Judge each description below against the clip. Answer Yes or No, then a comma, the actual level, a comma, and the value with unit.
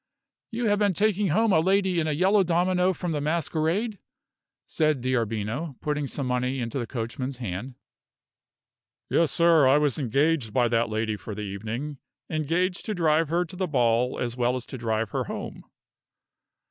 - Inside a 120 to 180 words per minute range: Yes, average, 170 wpm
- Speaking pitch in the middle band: Yes, medium, 150 Hz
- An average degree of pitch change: No, wide, 6.5 semitones